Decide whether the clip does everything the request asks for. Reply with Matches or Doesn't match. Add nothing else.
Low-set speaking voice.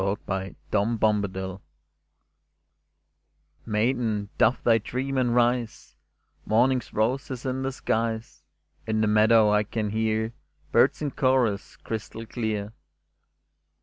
Matches